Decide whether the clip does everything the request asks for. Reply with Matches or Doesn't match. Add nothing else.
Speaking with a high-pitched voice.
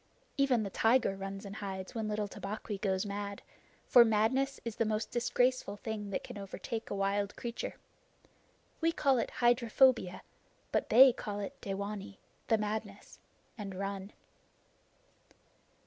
Matches